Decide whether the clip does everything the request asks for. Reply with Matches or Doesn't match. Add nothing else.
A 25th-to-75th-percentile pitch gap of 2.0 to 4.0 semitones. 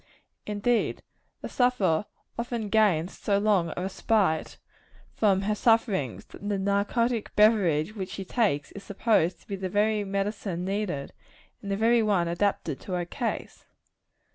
Matches